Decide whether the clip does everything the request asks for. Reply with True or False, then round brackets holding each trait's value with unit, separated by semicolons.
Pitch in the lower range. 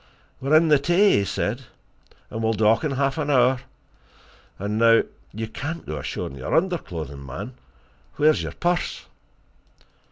True (125 Hz)